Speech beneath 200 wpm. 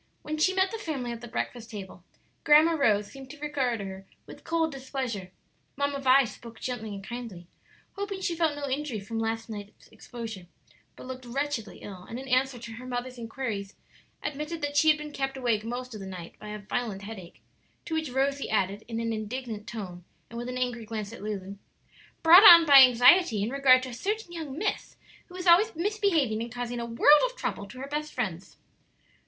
No: fast, 205 wpm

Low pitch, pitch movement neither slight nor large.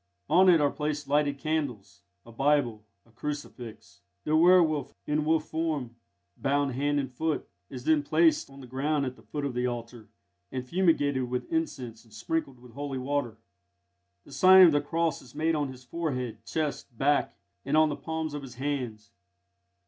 No: medium, 145 Hz; average, 3.8 semitones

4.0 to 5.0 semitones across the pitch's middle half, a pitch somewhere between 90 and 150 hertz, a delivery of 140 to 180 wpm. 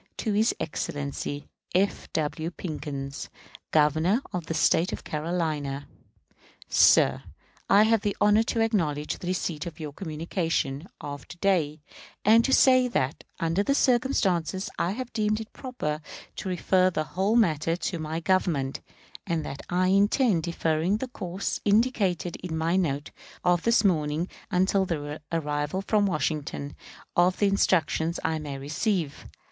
No: average, 4.7 semitones; medium, 175 Hz; average, 150 wpm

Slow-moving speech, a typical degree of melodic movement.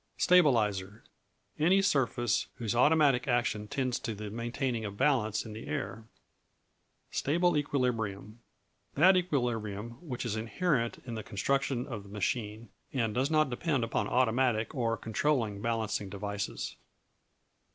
Yes: slow, 130 wpm; average, 4.2 semitones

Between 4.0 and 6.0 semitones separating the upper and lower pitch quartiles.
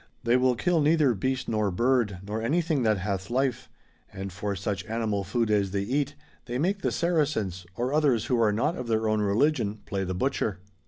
Yes: average, 4.8 semitones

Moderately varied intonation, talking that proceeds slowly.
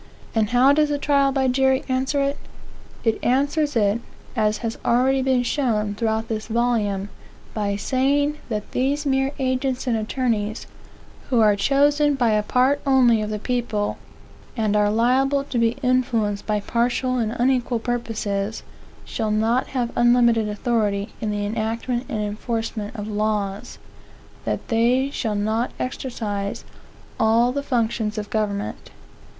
No: average, 3.4 semitones; average, 145 wpm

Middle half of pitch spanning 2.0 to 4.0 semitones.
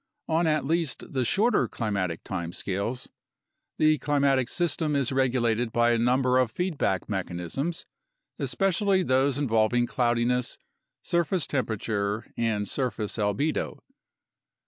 No: average, 5.2 semitones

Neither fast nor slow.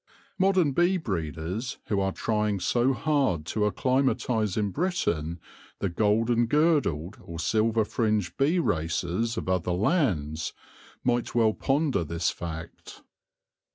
No: slow, 120 wpm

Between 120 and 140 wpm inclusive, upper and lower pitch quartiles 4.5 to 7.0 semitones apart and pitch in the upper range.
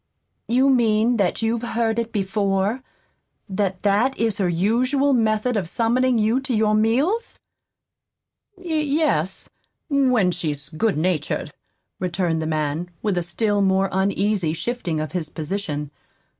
Yes: slow, 135 wpm; average, 4.9 semitones; high, 210 Hz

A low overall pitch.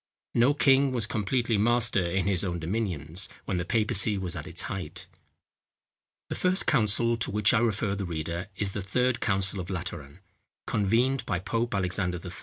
Yes: low, 100 Hz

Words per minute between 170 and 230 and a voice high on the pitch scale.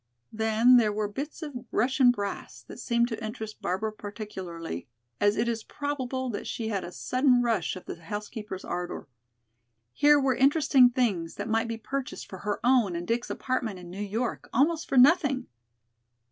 Yes: average, 175 wpm; high, 225 Hz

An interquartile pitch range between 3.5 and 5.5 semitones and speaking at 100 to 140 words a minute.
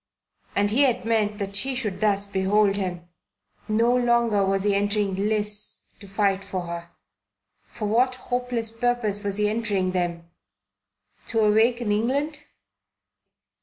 No: average, 2.9 semitones; slow, 135 wpm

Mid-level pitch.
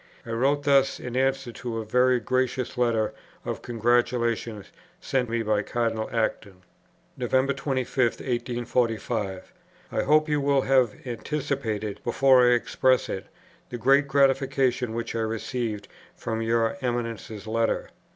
No: low, 120 Hz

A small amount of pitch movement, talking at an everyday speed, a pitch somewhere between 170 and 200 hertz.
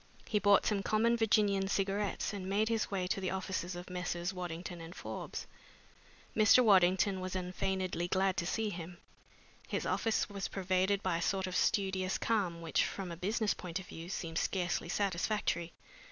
Yes: narrow, 2.2 semitones; average, 170 wpm; high, 190 Hz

